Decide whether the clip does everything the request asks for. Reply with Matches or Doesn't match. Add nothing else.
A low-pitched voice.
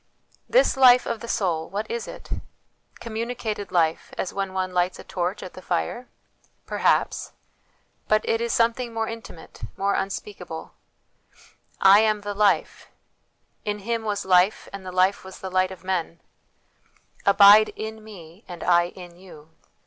Doesn't match